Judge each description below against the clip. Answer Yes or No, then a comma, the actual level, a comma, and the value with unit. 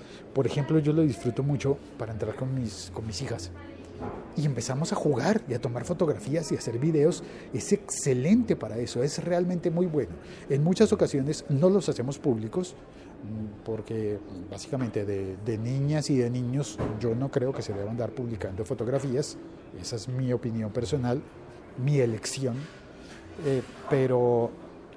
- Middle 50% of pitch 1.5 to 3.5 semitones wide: No, average, 4.6 semitones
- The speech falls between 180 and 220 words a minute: No, average, 160 wpm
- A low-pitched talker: Yes, low, 130 Hz